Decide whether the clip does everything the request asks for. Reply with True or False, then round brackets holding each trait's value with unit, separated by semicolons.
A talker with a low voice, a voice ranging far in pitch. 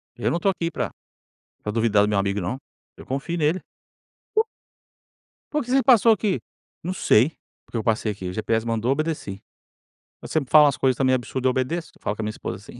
True (130 Hz; 7.4 semitones)